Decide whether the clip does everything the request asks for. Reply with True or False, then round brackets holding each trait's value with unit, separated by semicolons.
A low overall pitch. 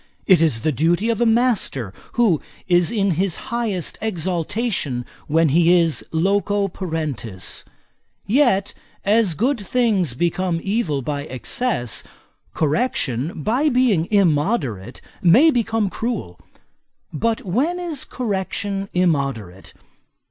False (185 Hz)